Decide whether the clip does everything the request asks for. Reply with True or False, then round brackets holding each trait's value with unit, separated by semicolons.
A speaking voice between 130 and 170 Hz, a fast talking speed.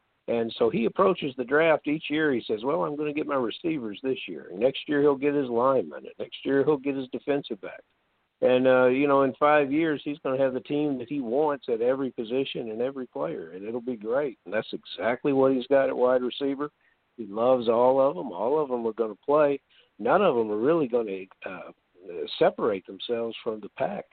True (135 Hz; 230 wpm)